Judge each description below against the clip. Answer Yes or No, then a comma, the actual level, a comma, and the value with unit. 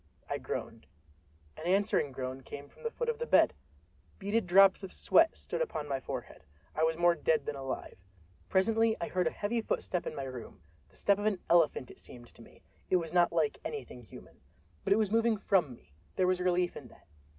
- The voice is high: No, medium, 175 Hz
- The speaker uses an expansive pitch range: Yes, wide, 6.9 semitones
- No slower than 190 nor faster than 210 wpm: Yes, average, 200 wpm